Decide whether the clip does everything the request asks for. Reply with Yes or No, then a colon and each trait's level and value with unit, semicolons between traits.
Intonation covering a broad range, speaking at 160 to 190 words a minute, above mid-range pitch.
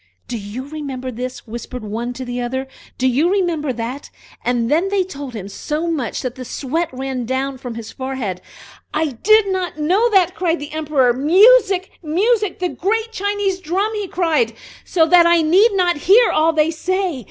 Yes: wide, 6.6 semitones; average, 180 wpm; very high, 310 Hz